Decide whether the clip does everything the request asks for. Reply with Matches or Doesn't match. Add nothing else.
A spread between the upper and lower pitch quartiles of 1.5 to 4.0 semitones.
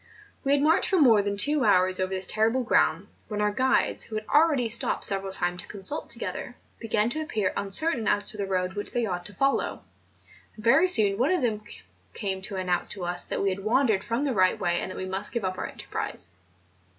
Doesn't match